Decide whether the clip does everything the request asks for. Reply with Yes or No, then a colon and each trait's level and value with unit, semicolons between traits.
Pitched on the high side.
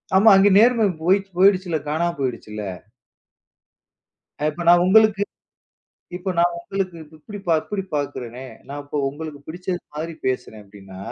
No: medium, 170 Hz